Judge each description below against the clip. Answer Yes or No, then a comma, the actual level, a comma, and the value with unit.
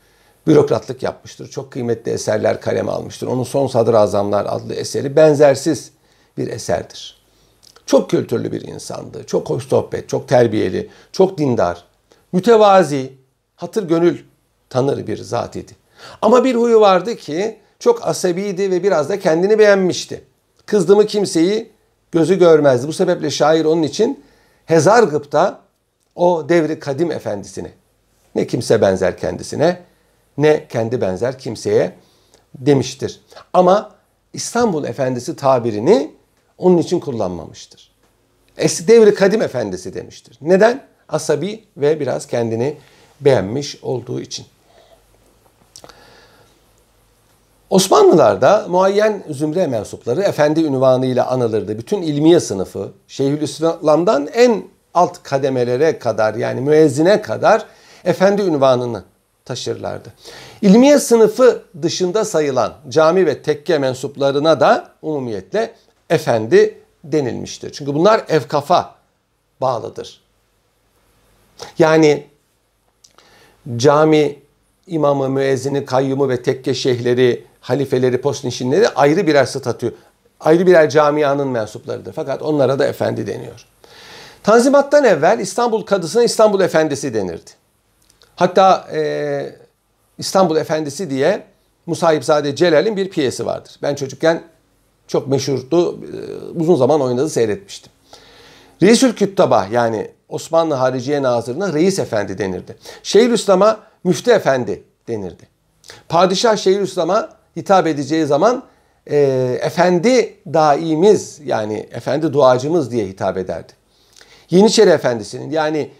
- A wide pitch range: Yes, wide, 6.5 semitones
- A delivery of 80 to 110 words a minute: Yes, average, 105 wpm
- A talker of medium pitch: Yes, medium, 155 Hz